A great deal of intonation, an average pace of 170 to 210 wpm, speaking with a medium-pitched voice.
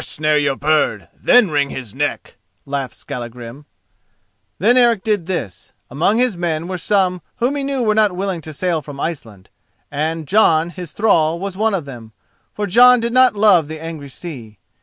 Yes: wide, 6.4 semitones; average, 180 wpm; medium, 170 Hz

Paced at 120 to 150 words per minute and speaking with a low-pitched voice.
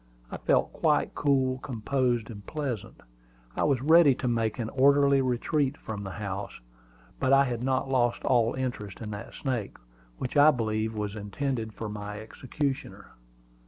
No: average, 160 wpm; low, 125 Hz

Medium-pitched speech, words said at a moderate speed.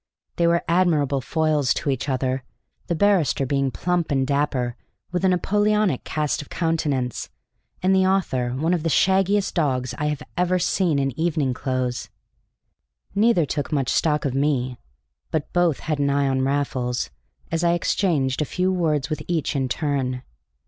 Yes: medium, 150 Hz; average, 165 wpm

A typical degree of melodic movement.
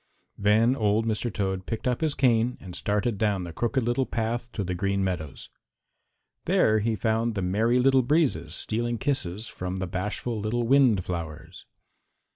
Yes: average, 3.8 semitones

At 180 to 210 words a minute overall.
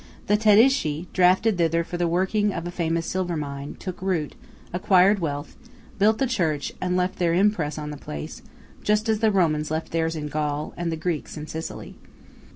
Yes: average, 185 wpm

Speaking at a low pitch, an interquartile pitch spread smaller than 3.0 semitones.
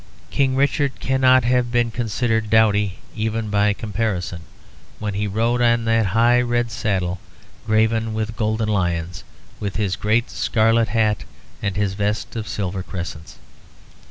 Yes: low, 110 Hz; narrow, 2.4 semitones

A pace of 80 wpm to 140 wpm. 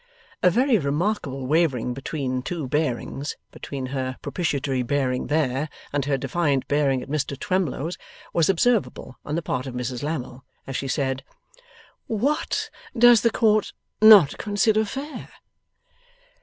Yes: slow, 135 wpm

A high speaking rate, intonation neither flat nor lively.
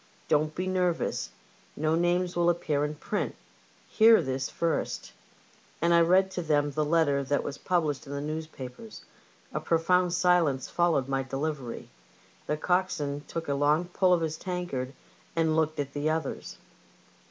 No: average, 160 wpm; average, 3.4 semitones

